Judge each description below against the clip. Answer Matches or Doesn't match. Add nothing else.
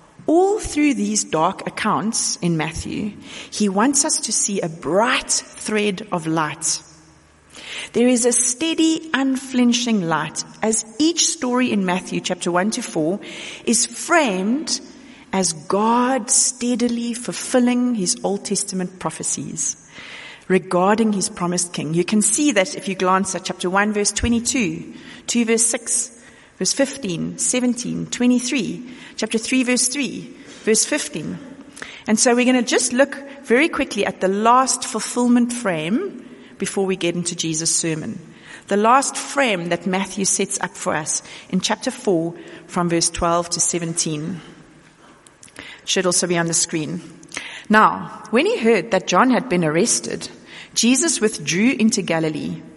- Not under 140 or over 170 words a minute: Matches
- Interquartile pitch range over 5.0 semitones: Matches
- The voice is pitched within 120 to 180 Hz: Doesn't match